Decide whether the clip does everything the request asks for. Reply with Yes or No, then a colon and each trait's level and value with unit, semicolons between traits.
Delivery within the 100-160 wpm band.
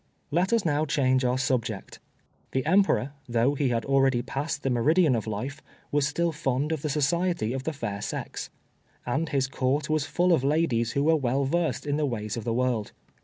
No: average, 200 wpm